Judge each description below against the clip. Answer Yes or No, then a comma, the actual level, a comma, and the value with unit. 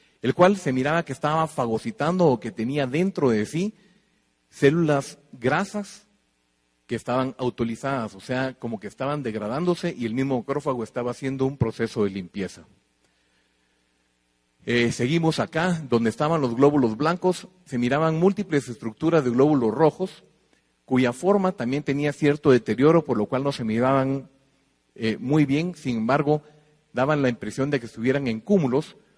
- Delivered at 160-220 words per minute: No, average, 150 wpm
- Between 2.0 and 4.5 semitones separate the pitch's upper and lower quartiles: No, average, 5.3 semitones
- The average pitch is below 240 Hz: Yes, low, 135 Hz